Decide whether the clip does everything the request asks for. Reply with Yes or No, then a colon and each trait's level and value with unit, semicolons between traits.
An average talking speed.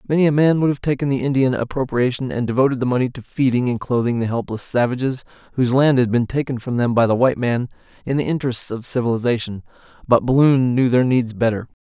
No: fast, 215 wpm